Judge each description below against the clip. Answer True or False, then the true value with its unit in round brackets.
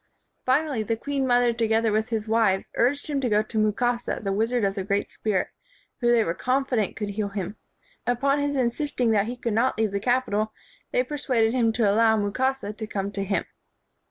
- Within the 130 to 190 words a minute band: False (205 wpm)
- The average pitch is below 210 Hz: False (225 Hz)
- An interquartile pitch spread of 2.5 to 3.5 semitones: True (3.1 semitones)